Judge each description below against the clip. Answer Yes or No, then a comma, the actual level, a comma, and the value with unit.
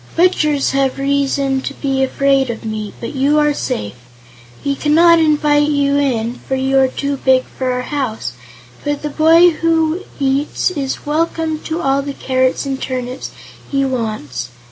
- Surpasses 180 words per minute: No, average, 165 wpm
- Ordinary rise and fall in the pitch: No, narrow, 2.3 semitones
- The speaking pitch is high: Yes, very high, 275 Hz